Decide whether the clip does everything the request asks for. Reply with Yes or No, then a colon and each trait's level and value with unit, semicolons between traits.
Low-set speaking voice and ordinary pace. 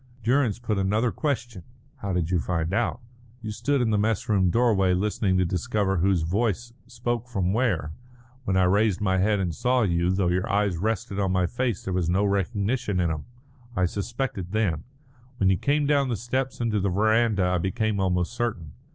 Yes: low, 100 Hz; average, 195 wpm